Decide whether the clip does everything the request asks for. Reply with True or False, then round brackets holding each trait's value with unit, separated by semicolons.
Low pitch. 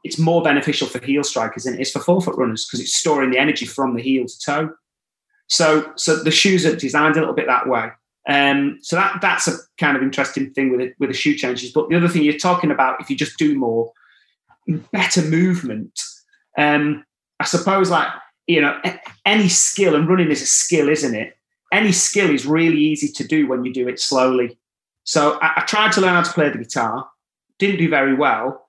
False (150 Hz)